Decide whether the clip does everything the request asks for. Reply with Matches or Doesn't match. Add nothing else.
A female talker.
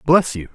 Doesn't match